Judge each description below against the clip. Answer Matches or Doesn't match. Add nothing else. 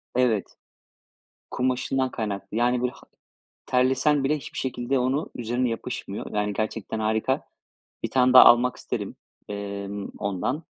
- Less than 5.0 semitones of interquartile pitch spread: Matches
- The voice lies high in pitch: Doesn't match